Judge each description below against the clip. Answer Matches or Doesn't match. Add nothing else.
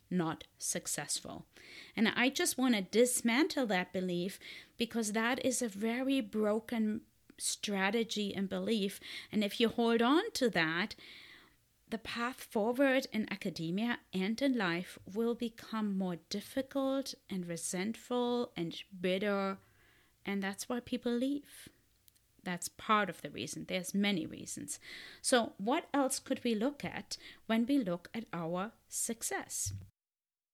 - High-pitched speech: Matches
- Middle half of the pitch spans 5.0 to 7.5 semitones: Doesn't match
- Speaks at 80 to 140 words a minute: Matches